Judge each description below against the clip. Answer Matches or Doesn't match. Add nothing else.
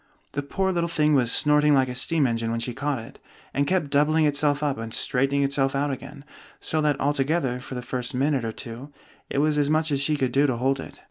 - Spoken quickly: Matches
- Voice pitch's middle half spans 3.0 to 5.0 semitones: Doesn't match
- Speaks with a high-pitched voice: Doesn't match